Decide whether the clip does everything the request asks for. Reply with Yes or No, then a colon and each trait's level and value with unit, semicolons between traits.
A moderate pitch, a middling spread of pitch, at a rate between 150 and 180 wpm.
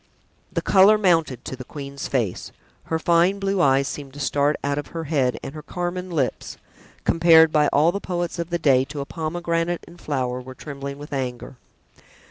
No: medium, 150 Hz; average, 3.8 semitones; average, 190 wpm